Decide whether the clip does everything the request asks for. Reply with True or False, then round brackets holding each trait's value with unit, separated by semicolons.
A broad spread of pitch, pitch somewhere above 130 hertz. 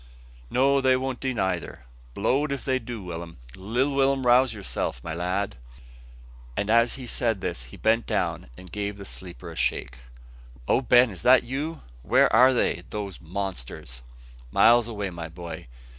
False (6.2 semitones; 110 Hz)